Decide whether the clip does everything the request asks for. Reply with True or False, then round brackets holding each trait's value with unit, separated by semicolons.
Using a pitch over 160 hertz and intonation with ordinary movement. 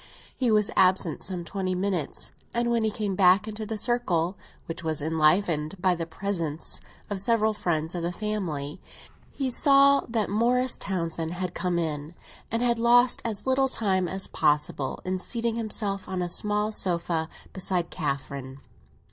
True (190 Hz; 4.6 semitones)